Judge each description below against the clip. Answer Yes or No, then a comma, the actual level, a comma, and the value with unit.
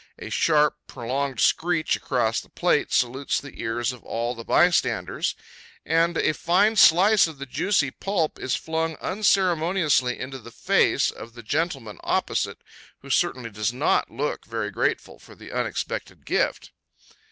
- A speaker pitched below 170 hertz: Yes, medium, 140 Hz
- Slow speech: No, average, 145 wpm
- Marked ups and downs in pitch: Yes, wide, 6.0 semitones